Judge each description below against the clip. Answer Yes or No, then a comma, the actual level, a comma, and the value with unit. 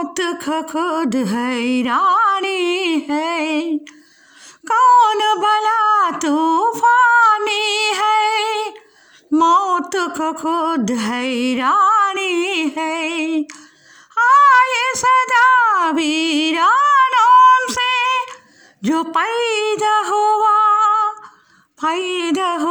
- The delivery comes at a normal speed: No, slow, 60 wpm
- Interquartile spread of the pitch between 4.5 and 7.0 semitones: Yes, average, 5.1 semitones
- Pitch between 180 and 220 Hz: No, very high, 380 Hz